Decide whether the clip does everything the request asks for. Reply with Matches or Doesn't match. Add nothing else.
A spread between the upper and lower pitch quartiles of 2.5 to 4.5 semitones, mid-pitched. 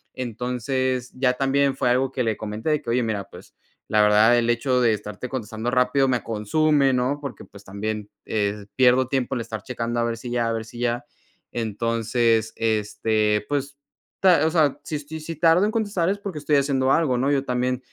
Doesn't match